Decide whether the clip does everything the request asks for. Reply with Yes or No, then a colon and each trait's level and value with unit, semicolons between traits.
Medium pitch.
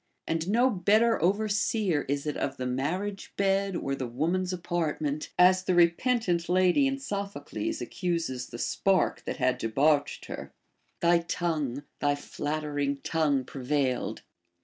Yes: medium, 170 Hz